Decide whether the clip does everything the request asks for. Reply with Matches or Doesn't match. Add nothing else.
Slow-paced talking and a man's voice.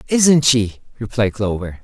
Matches